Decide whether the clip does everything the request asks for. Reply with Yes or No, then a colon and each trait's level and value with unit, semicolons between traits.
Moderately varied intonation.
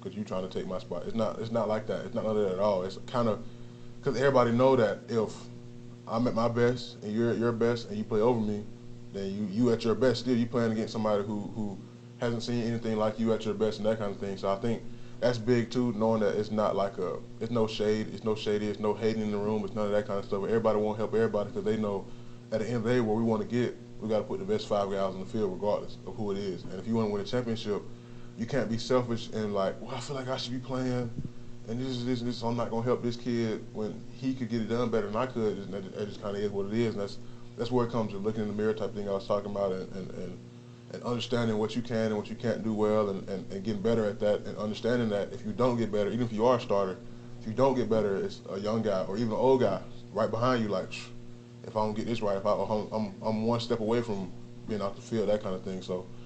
No: narrow, 2.3 semitones